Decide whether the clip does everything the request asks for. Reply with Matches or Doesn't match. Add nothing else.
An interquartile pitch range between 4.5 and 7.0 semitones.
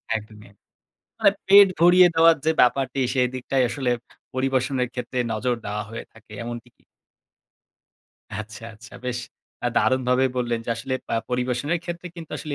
Doesn't match